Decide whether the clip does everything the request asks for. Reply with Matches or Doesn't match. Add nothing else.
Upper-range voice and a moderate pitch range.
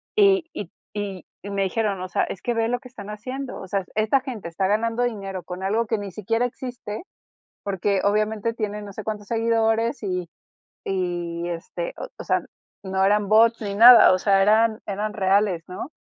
Matches